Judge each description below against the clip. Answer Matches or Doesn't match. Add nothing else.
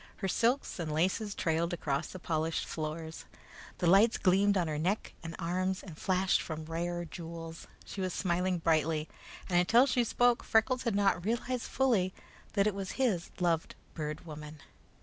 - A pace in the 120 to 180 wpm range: Matches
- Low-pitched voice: Doesn't match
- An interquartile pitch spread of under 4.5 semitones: Matches